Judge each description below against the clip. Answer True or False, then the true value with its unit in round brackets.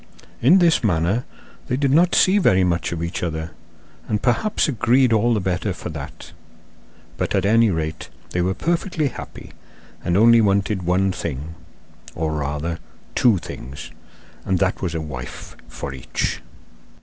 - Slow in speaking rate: False (155 wpm)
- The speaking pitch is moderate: False (95 Hz)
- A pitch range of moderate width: False (6.3 semitones)